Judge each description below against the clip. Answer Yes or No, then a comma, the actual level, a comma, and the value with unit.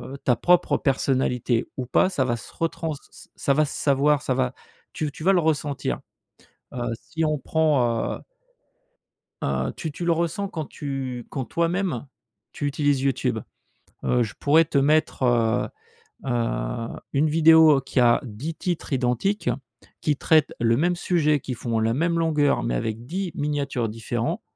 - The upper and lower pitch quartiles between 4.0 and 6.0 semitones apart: Yes, average, 4.6 semitones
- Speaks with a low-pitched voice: No, medium, 145 Hz